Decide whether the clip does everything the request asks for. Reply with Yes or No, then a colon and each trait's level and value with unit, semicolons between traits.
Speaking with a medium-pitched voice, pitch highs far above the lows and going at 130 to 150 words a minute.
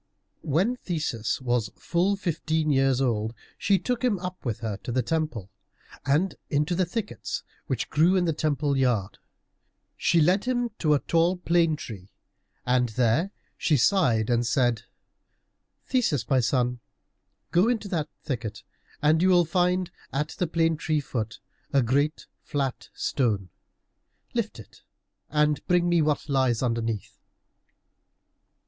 Yes: medium, 150 Hz; wide, 6.1 semitones; average, 140 wpm